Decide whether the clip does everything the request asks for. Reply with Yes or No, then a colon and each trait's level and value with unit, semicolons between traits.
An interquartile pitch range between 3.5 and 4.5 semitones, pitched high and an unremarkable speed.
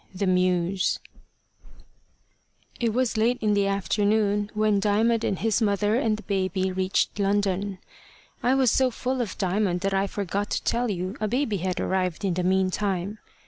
No: narrow, 2.5 semitones; high, 200 Hz; average, 165 wpm